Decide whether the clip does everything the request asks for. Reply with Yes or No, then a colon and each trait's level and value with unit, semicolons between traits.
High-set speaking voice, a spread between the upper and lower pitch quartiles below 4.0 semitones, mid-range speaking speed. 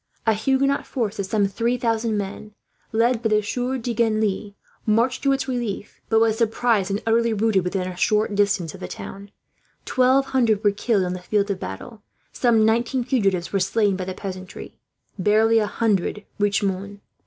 Yes: high, 215 Hz; average, 2.8 semitones; average, 180 wpm